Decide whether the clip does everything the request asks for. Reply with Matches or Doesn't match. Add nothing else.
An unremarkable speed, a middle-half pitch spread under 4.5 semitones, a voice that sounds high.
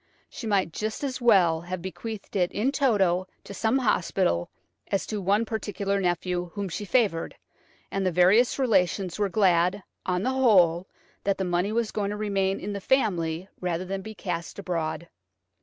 Matches